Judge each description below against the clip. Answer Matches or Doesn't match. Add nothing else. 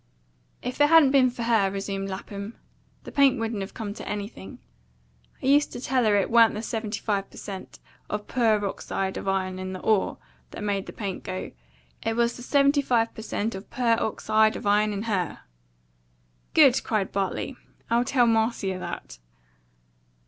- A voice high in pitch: Matches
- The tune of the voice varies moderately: Matches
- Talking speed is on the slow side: Doesn't match